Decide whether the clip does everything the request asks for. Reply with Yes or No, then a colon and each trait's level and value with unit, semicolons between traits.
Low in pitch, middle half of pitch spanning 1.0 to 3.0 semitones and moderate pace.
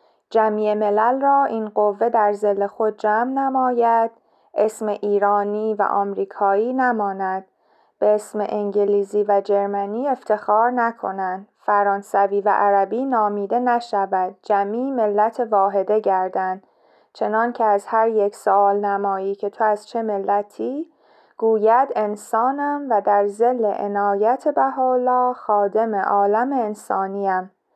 No: high, 210 Hz; narrow, 2.4 semitones; average, 115 wpm